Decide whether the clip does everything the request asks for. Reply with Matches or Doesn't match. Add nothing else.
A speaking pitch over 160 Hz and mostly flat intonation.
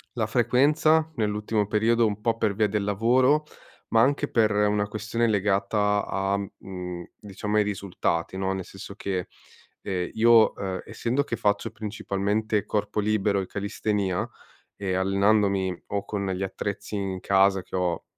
Doesn't match